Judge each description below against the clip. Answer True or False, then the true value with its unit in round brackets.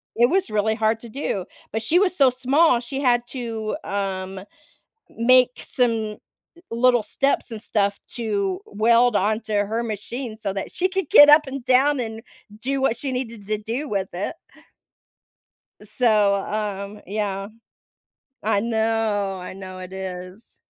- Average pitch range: True (3.7 semitones)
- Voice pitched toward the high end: True (220 Hz)